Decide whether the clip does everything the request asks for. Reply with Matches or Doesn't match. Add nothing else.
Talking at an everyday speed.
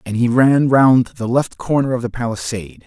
Doesn't match